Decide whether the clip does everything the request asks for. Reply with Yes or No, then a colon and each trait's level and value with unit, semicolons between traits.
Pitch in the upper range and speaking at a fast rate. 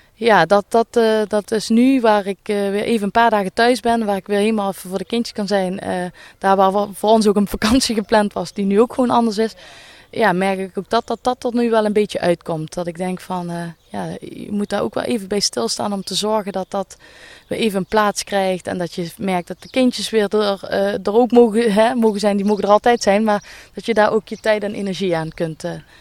Yes: high, 205 Hz; fast, 260 wpm